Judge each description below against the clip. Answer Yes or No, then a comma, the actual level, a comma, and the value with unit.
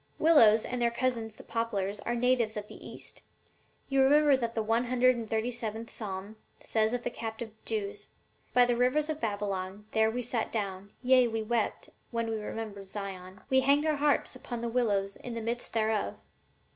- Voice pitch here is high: Yes, high, 230 Hz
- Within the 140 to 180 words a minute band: No, average, 190 wpm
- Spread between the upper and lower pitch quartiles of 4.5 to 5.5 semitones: No, average, 2.8 semitones